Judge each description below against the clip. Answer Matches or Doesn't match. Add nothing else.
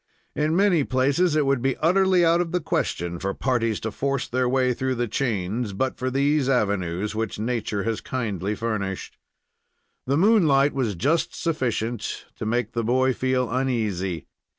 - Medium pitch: Doesn't match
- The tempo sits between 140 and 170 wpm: Matches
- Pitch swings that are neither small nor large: Matches